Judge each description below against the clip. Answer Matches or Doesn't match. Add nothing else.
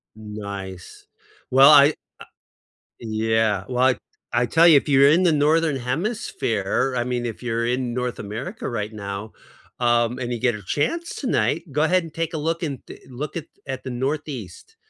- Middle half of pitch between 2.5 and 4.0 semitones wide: Doesn't match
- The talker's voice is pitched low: Matches